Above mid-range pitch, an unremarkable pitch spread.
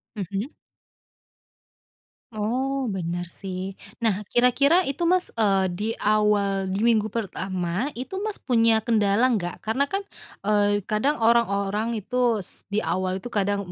Yes: high, 210 Hz; average, 3.6 semitones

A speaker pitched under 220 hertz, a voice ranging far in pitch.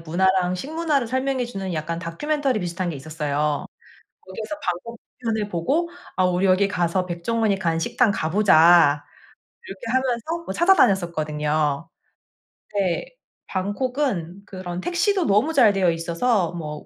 Yes: high, 190 Hz; wide, 6.3 semitones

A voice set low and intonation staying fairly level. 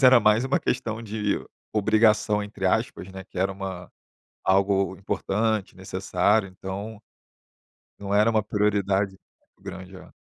Yes: low, 100 Hz; narrow, 2.2 semitones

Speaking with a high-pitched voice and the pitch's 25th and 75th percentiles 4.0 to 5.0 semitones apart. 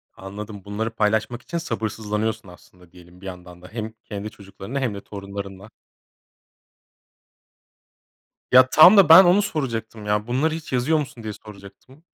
No: low, 110 Hz; average, 4.5 semitones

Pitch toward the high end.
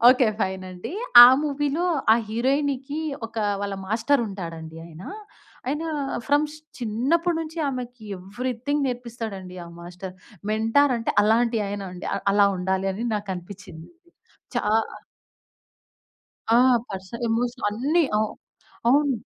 Yes: high, 230 Hz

